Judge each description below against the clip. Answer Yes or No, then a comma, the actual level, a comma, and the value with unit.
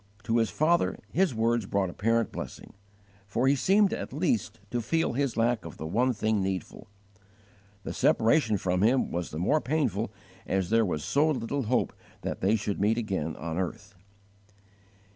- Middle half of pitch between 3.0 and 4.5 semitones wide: No, average, 4.9 semitones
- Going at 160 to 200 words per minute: Yes, average, 170 wpm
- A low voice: Yes, low, 115 Hz